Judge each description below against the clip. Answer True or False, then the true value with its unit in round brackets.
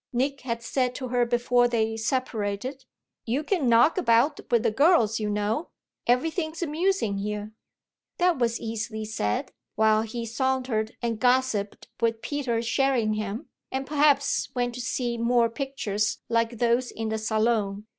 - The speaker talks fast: False (145 wpm)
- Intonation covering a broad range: False (3.2 semitones)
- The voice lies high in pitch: True (235 Hz)